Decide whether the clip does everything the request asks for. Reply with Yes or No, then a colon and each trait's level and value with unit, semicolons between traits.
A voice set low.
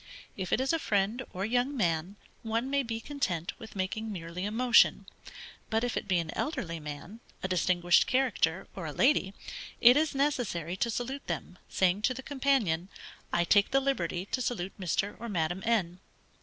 No: high, 210 Hz